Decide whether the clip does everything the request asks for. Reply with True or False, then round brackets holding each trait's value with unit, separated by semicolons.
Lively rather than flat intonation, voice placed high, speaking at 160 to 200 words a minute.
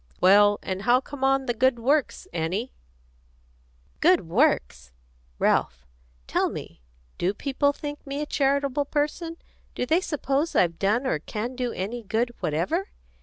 False (6.2 semitones; 250 Hz; 150 wpm)